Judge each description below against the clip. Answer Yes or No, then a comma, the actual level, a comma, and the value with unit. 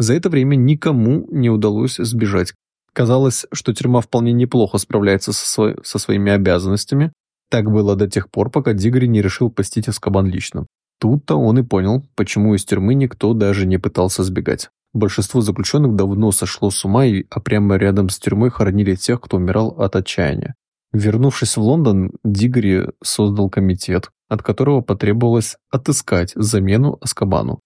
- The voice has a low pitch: Yes, low, 105 Hz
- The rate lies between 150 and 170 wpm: Yes, average, 155 wpm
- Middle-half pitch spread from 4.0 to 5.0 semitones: No, average, 3.5 semitones